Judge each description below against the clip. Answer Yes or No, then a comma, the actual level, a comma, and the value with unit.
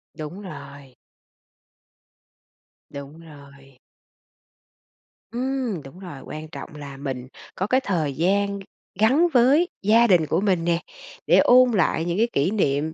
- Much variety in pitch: Yes, wide, 7.1 semitones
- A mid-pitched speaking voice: Yes, medium, 175 Hz